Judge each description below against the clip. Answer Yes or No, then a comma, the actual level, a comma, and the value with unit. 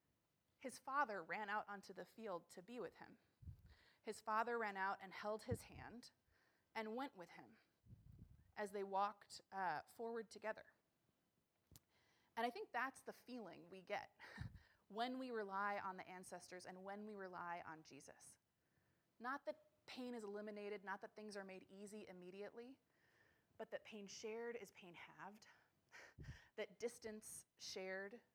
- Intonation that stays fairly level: No, average, 3.2 semitones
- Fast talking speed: No, average, 150 wpm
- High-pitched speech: Yes, high, 210 Hz